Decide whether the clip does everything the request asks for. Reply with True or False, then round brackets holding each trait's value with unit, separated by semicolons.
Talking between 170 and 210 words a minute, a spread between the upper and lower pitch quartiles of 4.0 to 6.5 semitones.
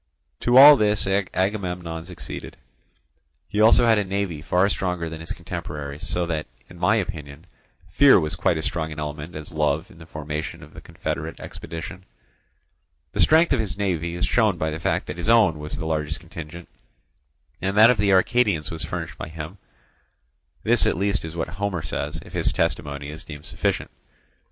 True (185 wpm; 4.3 semitones)